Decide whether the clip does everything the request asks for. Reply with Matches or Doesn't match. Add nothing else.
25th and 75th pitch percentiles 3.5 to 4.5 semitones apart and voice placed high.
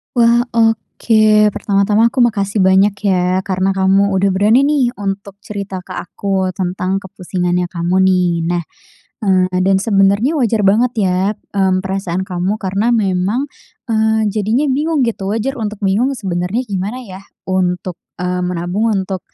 Doesn't match